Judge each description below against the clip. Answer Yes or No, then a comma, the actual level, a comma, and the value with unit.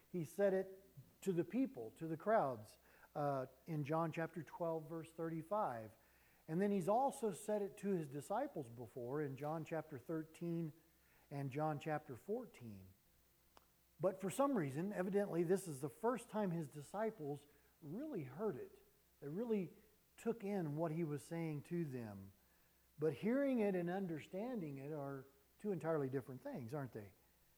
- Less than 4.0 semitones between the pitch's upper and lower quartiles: No, wide, 5.6 semitones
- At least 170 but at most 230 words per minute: No, average, 155 wpm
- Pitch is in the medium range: Yes, medium, 165 Hz